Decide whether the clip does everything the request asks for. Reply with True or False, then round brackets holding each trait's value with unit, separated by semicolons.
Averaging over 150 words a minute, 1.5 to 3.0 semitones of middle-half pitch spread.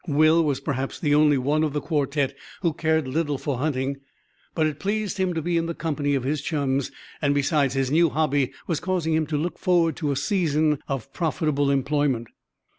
True (200 wpm; 2.6 semitones)